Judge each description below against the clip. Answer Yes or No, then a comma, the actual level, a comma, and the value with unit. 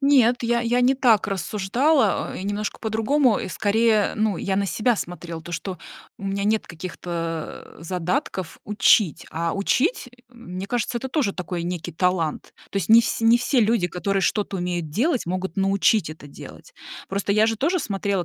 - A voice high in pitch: Yes, high, 200 Hz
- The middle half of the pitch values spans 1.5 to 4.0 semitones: No, average, 4.5 semitones